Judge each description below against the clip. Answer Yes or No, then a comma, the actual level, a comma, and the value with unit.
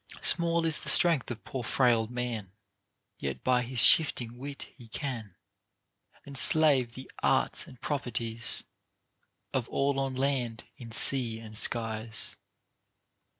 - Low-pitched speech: Yes, low, 125 Hz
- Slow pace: Yes, slow, 125 wpm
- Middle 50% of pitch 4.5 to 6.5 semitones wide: No, average, 3.1 semitones